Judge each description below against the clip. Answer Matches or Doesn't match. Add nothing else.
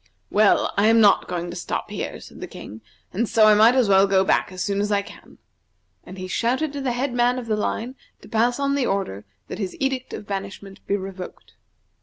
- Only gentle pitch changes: Doesn't match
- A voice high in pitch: Matches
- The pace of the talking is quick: Matches